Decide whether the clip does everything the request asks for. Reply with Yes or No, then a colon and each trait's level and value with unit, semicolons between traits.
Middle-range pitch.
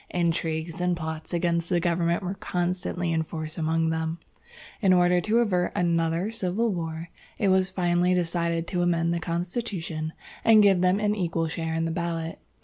Yes: medium, 175 Hz